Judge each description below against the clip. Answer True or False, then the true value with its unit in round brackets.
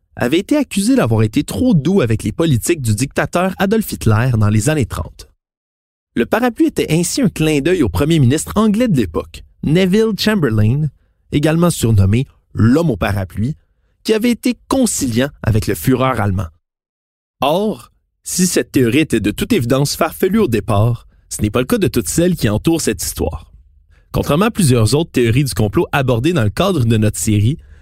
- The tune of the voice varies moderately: False (8.6 semitones)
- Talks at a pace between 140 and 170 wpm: False (180 wpm)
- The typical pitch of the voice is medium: False (125 Hz)